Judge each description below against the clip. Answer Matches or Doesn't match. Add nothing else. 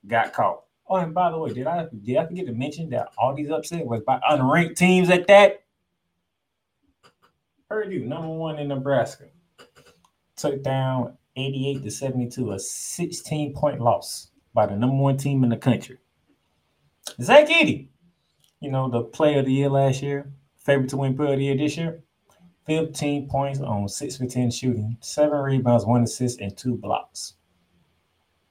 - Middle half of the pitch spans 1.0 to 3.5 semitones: Doesn't match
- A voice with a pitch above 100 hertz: Matches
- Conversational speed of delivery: Matches